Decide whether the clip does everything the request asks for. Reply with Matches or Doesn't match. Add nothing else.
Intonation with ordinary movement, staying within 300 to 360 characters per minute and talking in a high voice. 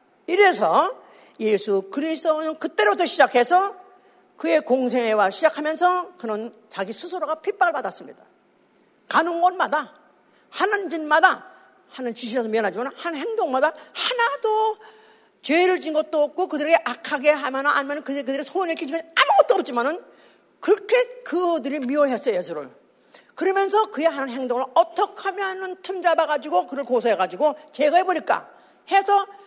Matches